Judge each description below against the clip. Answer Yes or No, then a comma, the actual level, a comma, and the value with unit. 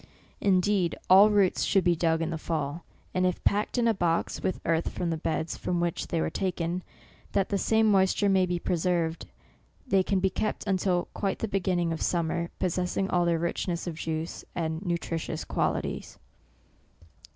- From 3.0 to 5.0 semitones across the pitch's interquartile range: No, narrow, 2.4 semitones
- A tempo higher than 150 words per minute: Yes, average, 175 wpm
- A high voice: No, medium, 175 Hz